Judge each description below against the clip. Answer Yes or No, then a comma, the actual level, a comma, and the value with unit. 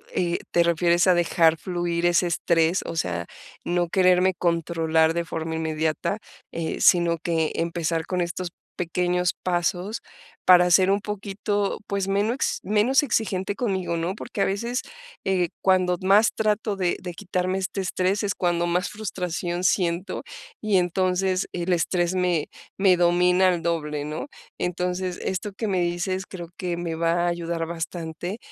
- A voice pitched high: No, medium, 180 Hz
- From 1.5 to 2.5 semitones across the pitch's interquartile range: Yes, narrow, 1.9 semitones